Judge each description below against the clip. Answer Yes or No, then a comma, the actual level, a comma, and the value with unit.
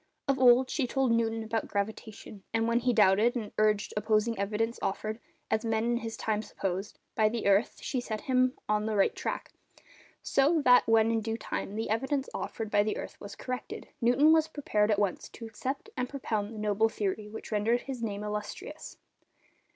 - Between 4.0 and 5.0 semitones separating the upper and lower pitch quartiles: No, average, 2.7 semitones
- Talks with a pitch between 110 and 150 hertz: No, high, 225 Hz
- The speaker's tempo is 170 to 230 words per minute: Yes, average, 185 wpm